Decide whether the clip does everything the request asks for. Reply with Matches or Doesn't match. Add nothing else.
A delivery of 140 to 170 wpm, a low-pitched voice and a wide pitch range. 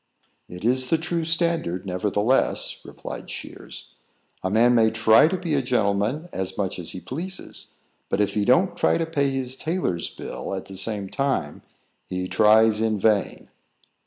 Matches